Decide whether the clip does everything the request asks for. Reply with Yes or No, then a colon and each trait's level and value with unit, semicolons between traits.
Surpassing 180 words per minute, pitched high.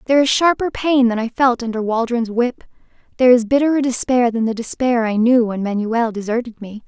Yes: average, 200 wpm; high, 240 Hz